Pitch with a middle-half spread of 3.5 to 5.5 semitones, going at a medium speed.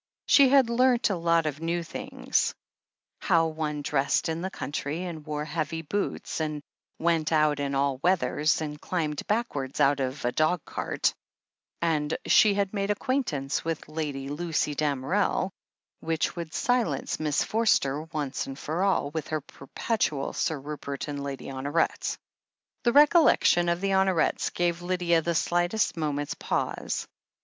Yes: average, 3.8 semitones; average, 155 wpm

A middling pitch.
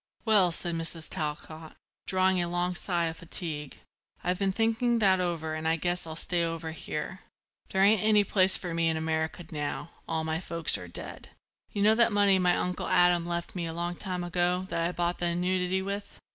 Yes: medium, 175 Hz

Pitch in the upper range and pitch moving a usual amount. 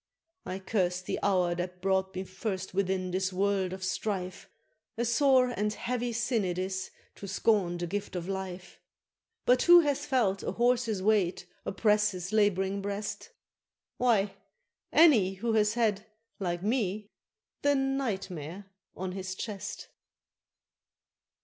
Yes: high, 195 Hz; average, 3.2 semitones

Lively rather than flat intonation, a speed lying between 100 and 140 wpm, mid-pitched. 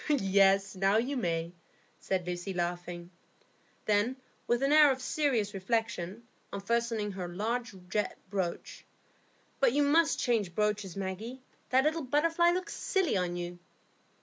No: wide, 5.7 semitones; slow, 135 wpm; high, 210 Hz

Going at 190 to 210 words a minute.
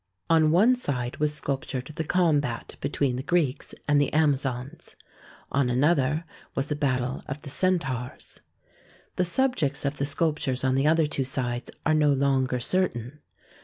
No: average, 160 wpm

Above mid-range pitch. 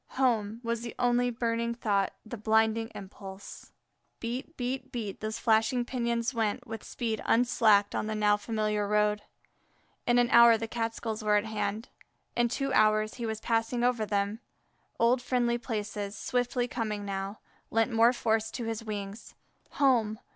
Yes: high, 225 Hz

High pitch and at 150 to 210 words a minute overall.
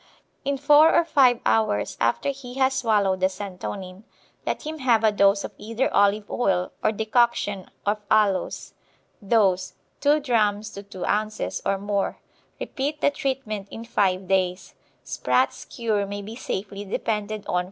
Yes: high, 210 Hz; average, 160 wpm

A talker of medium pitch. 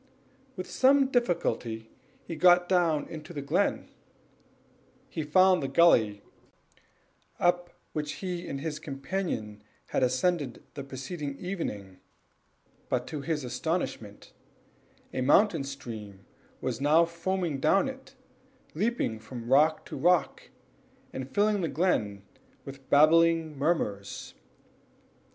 Yes: medium, 155 Hz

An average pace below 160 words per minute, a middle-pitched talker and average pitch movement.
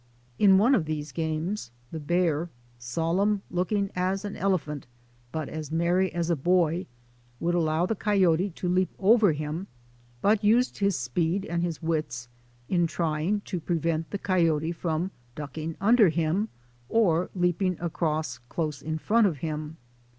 Yes: average, 150 wpm; medium, 170 Hz; average, 3.4 semitones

